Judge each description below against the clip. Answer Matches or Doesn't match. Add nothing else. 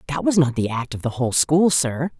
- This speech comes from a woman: Matches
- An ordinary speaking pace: Doesn't match